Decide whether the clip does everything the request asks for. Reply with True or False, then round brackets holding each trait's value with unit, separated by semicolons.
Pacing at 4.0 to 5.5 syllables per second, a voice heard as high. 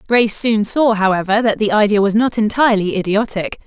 False (5.8 syllables/s; 210 Hz)